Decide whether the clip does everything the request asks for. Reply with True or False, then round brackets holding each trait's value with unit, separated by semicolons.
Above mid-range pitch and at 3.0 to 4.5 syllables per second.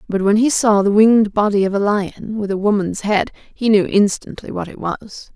False (205 Hz; 5.0 syllables/s)